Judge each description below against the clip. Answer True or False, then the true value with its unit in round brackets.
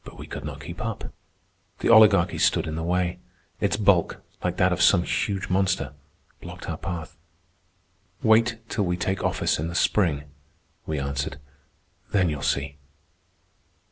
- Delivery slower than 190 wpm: True (155 wpm)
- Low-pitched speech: True (90 Hz)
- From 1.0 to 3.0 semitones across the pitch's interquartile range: False (4.1 semitones)